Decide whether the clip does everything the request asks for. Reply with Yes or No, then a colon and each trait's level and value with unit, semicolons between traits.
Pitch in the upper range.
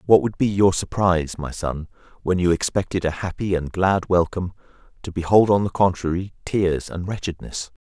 No: very low, 90 Hz